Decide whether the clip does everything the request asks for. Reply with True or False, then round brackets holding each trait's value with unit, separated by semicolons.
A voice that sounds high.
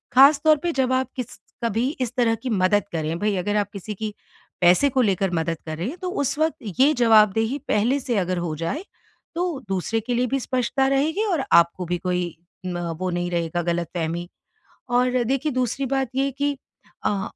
True (225 Hz)